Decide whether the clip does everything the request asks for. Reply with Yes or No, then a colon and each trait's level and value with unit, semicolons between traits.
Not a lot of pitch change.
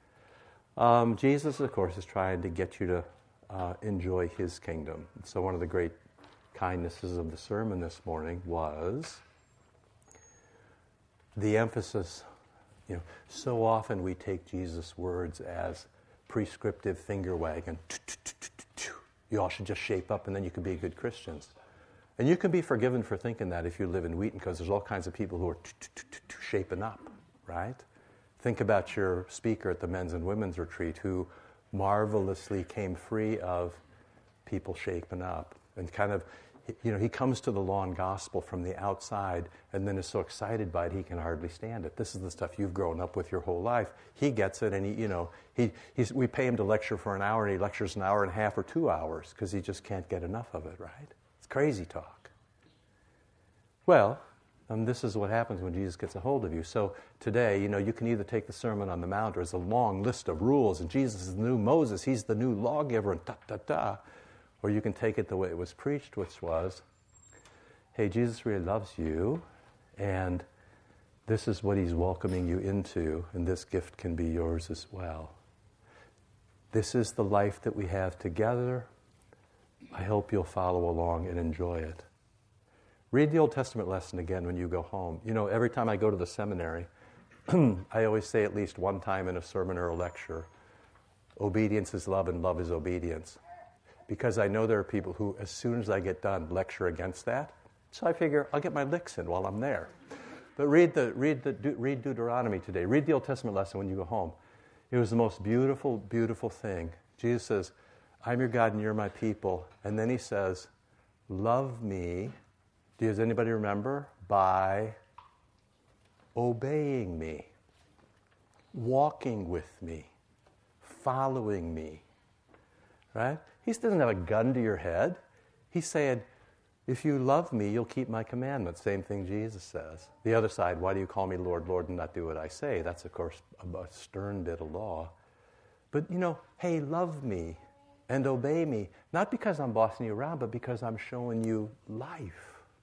No: average, 4.0 semitones